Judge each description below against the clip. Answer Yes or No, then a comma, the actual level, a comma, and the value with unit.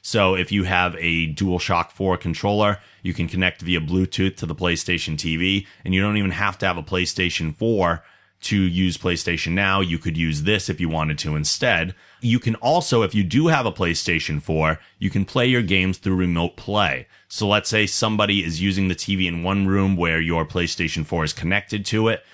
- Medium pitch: No, very low, 95 Hz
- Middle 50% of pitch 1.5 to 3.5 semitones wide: Yes, average, 3.2 semitones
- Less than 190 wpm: No, fast, 205 wpm